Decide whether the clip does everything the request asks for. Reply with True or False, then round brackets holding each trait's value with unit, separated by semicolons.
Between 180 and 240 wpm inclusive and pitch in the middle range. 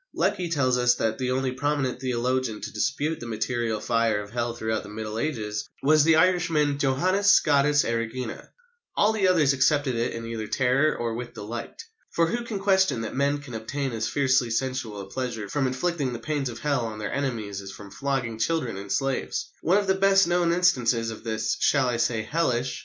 False (200 wpm; 130 Hz)